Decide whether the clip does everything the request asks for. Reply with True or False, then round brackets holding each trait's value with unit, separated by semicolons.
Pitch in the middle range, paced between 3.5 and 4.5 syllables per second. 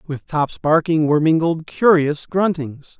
True (160 Hz; 4.2 syllables/s)